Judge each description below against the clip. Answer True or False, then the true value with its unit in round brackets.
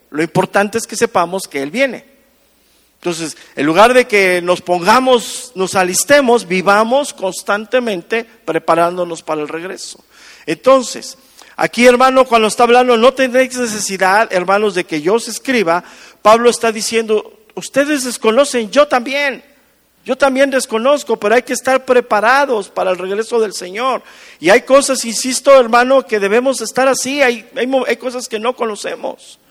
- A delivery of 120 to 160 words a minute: True (150 wpm)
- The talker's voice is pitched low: False (230 Hz)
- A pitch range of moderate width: True (4.9 semitones)